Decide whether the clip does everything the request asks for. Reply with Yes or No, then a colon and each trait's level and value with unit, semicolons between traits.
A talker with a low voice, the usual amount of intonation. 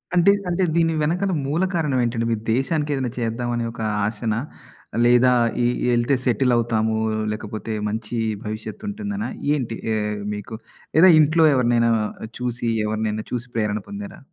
No: low, 120 Hz; wide, 6.0 semitones